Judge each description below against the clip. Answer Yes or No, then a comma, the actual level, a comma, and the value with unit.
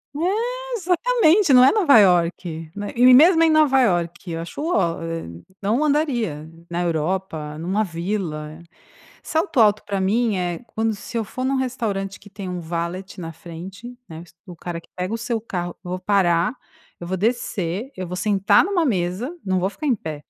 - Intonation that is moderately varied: No, wide, 6.5 semitones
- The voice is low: No, high, 195 Hz